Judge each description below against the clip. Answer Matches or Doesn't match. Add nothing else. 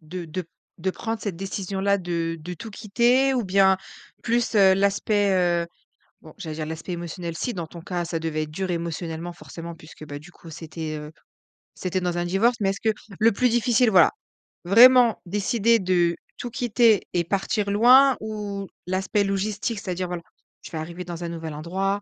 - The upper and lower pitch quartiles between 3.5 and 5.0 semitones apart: Matches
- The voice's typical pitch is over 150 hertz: Matches